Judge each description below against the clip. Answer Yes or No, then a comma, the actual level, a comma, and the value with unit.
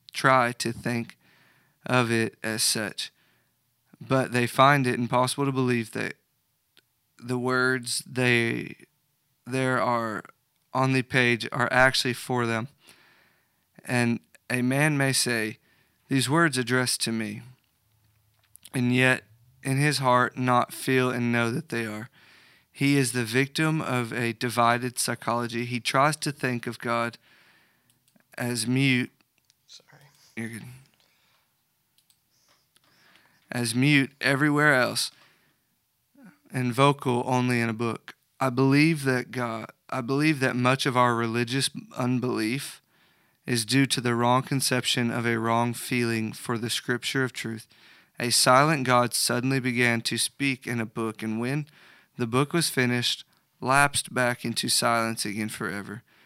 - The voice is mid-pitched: No, low, 125 Hz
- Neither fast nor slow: No, slow, 130 wpm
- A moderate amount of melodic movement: No, narrow, 2.1 semitones